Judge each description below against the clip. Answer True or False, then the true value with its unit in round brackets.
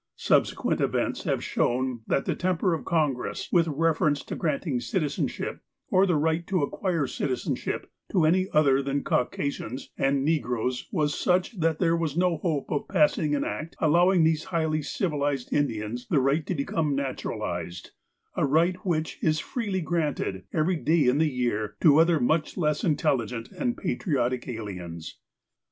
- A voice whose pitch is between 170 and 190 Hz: False (150 Hz)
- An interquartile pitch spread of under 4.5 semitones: True (3.9 semitones)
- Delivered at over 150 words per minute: True (160 wpm)